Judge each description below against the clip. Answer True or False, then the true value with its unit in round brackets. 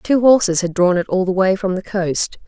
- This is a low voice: False (190 Hz)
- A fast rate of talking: True (265 wpm)